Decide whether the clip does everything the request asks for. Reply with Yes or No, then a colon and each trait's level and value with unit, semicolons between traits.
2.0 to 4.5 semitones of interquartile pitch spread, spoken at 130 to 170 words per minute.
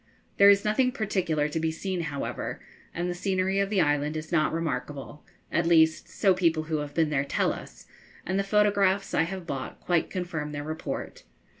No: average, 4.0 semitones; average, 190 wpm